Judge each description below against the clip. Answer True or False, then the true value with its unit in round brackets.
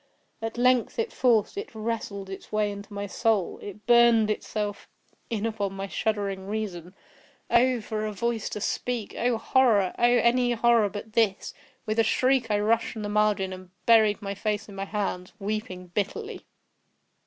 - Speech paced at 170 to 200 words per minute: False (155 wpm)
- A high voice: True (215 Hz)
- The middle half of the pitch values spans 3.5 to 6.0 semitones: False (2.5 semitones)